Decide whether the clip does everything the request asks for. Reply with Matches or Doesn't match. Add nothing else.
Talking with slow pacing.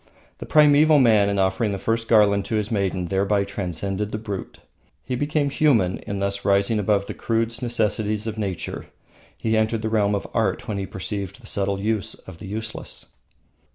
Doesn't match